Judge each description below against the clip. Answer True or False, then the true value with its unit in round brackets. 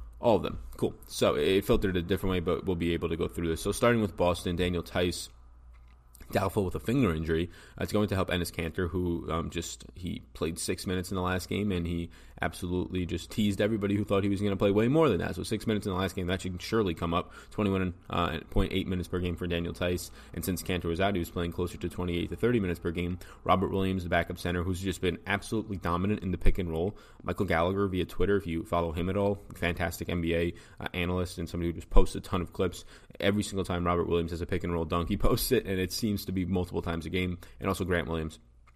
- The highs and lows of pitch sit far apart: False (2.5 semitones)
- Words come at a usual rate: False (255 wpm)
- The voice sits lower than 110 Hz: True (90 Hz)